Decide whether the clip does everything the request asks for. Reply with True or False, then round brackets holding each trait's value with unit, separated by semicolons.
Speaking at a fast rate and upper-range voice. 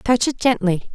False (190 wpm; 220 Hz)